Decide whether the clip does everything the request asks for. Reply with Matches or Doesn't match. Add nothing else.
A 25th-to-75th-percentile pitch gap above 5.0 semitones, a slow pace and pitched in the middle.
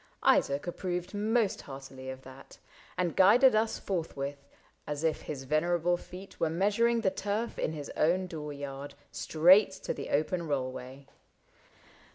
Doesn't match